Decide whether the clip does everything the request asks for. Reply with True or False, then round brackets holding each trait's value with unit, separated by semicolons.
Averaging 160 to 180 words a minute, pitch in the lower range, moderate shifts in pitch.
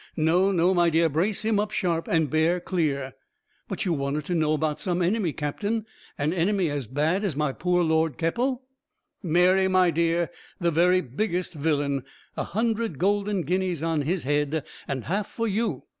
False (175 wpm; 170 Hz; 3.6 semitones)